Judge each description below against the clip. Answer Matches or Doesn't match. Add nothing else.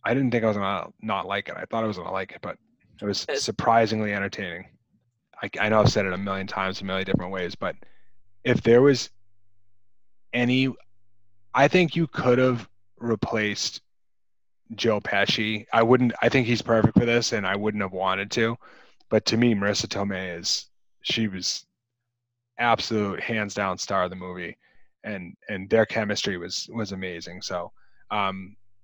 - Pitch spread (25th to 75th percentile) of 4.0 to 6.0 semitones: Doesn't match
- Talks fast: Doesn't match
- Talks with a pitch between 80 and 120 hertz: Matches